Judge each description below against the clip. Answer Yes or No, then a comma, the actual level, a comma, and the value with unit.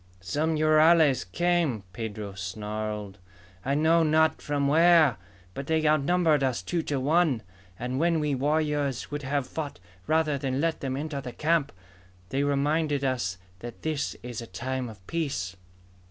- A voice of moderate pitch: Yes, medium, 145 Hz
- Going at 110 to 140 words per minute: No, average, 155 wpm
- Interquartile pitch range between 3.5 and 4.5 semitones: Yes, average, 4.1 semitones